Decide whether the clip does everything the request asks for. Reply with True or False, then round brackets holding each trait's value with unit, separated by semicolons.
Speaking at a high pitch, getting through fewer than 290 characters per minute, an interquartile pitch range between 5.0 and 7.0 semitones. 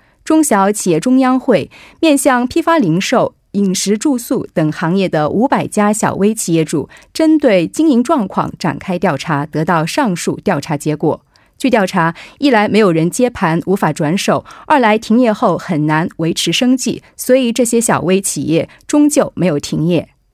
False (205 Hz; 255 characters per minute; 7.4 semitones)